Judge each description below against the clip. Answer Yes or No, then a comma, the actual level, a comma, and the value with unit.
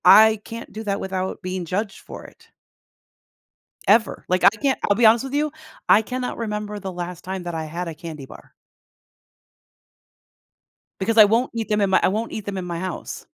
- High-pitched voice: Yes, high, 200 Hz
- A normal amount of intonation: Yes, average, 3.3 semitones